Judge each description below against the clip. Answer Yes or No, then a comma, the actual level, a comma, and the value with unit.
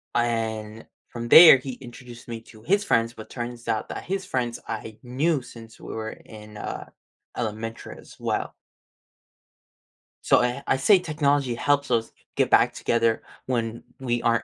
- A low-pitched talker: Yes, low, 120 Hz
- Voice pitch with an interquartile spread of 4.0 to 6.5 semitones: No, average, 2.8 semitones